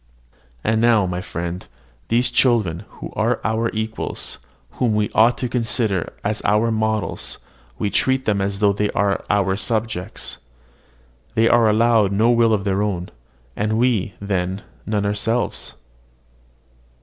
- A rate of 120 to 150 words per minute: Yes, average, 145 wpm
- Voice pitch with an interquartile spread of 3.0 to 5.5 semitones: No, narrow, 2.4 semitones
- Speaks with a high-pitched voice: No, low, 105 Hz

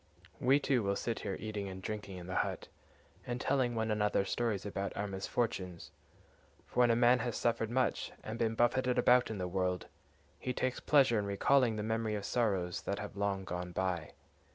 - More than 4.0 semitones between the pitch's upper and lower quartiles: No, average, 3.7 semitones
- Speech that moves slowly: No, average, 195 wpm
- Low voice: Yes, low, 110 Hz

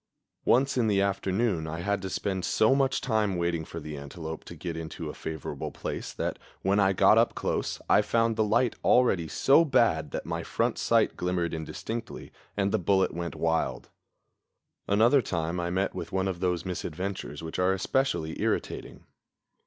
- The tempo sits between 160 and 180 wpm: Yes, average, 175 wpm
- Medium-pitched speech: No, very low, 95 Hz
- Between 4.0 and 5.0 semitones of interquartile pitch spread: Yes, average, 4.7 semitones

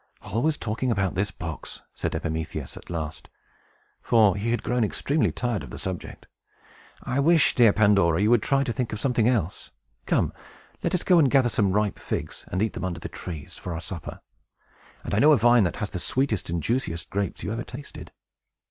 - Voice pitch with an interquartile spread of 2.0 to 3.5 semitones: No, average, 5.1 semitones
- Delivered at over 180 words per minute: Yes, average, 200 wpm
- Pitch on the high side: No, low, 105 Hz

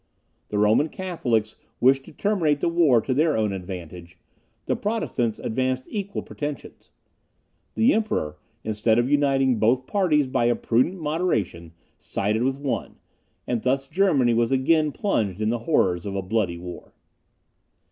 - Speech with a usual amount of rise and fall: No, wide, 5.9 semitones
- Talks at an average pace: Yes, average, 145 wpm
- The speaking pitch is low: Yes, low, 130 Hz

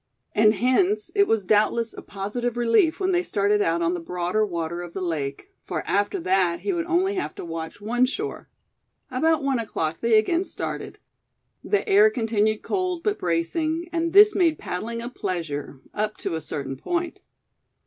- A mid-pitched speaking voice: No, high, 225 Hz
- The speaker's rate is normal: Yes, average, 180 wpm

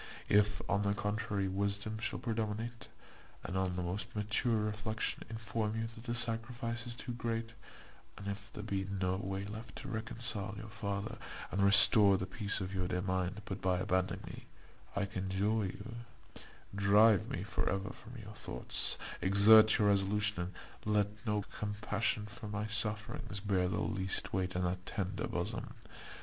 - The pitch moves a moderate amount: No, narrow, 2.2 semitones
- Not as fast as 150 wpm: No, average, 165 wpm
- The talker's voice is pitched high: No, low, 105 Hz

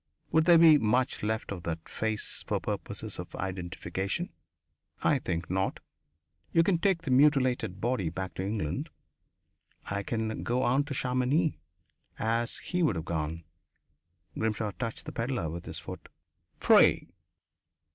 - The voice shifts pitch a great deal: Yes, wide, 5.8 semitones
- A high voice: No, low, 110 Hz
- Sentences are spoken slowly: No, average, 145 wpm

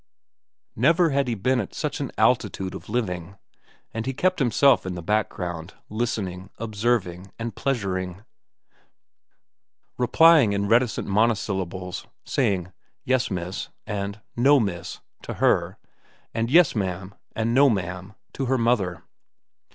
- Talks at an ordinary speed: No, slow, 130 wpm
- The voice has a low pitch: Yes, low, 105 Hz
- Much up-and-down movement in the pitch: No, average, 4.7 semitones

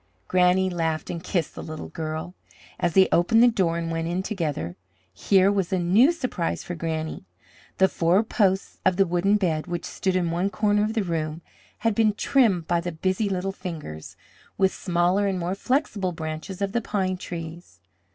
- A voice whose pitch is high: No, medium, 180 Hz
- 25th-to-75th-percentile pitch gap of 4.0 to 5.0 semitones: No, average, 2.9 semitones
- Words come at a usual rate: Yes, average, 185 wpm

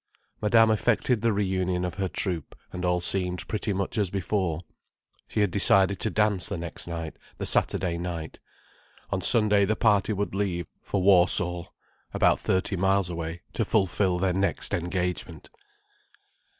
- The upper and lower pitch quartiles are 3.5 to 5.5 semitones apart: No, narrow, 2.5 semitones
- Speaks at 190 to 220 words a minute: No, average, 150 wpm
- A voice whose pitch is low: Yes, very low, 95 Hz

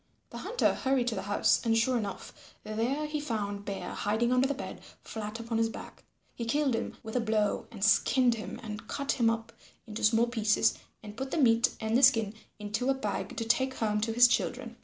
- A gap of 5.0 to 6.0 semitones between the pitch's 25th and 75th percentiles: No, average, 2.8 semitones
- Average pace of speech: No, fast, 215 wpm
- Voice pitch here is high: Yes, high, 230 Hz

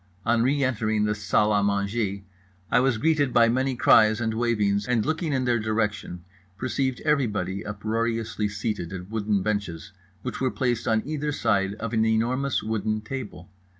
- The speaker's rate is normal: Yes, average, 165 wpm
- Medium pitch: No, low, 110 Hz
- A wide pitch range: No, average, 3.1 semitones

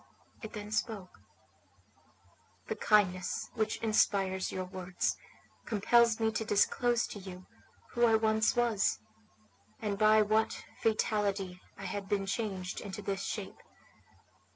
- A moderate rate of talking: No, slow, 125 wpm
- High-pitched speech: Yes, high, 210 Hz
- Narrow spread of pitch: Yes, narrow, 2.3 semitones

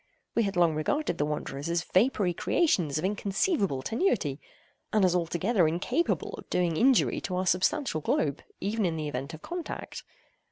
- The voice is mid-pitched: Yes, medium, 180 Hz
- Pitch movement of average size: No, wide, 6.0 semitones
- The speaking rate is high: No, average, 165 wpm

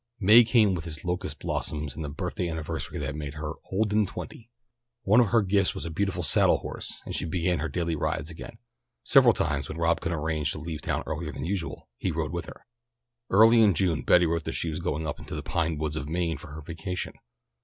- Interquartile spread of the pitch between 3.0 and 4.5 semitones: Yes, average, 3.5 semitones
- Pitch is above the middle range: No, very low, 85 Hz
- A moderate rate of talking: No, fast, 230 wpm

